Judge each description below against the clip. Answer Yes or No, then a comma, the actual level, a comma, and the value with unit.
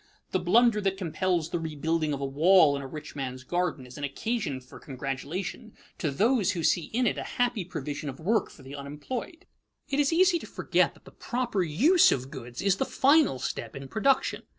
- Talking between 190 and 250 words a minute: Yes, fast, 205 wpm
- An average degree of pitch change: No, wide, 8.6 semitones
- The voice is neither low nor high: Yes, medium, 170 Hz